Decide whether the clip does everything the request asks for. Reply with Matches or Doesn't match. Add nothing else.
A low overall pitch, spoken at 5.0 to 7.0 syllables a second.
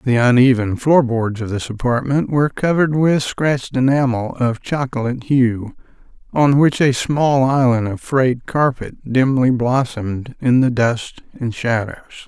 Doesn't match